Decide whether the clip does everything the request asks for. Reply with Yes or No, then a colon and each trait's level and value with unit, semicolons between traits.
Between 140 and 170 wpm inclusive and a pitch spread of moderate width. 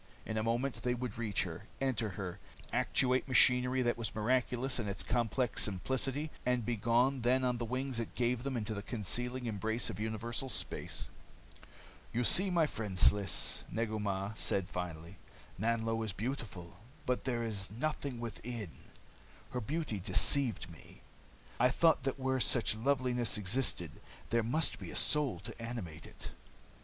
Yes: average, 160 wpm; average, 3.3 semitones